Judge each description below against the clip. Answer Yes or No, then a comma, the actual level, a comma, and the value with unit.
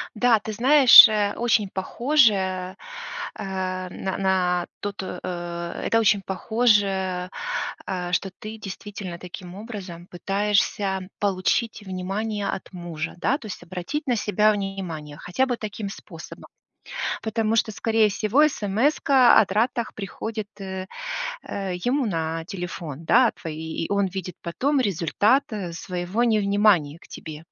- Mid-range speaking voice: No, high, 195 Hz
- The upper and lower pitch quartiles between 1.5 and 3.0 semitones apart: No, average, 3.4 semitones